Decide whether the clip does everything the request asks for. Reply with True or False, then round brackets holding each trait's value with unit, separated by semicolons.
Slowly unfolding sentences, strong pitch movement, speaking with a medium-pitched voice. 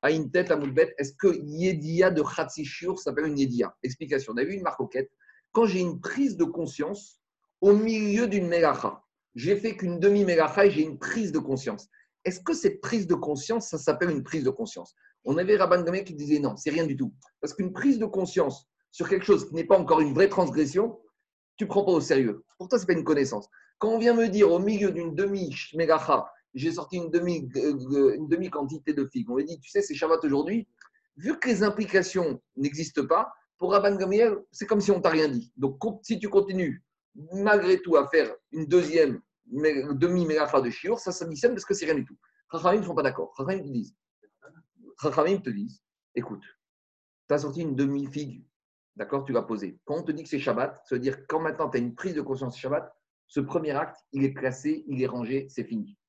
False (215 wpm; 5.8 semitones; 170 Hz)